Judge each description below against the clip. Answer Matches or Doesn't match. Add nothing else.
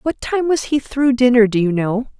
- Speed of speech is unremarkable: Doesn't match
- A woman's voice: Matches